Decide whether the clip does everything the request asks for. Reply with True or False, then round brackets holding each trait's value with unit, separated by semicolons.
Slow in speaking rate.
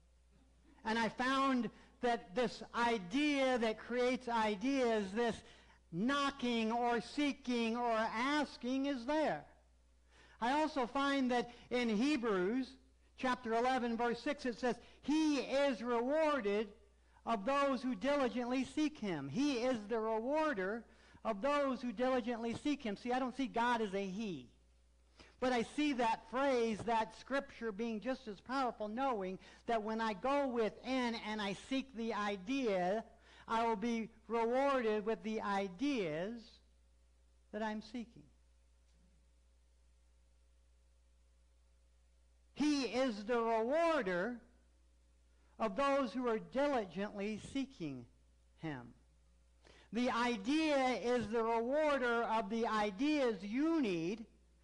True (120 wpm)